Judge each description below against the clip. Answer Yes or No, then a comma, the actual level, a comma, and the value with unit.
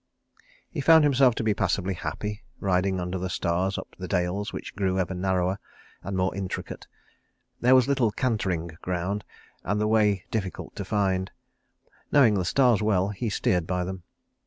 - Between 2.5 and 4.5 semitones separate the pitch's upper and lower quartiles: Yes, average, 2.8 semitones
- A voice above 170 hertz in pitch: No, very low, 95 Hz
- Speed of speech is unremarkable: Yes, average, 165 wpm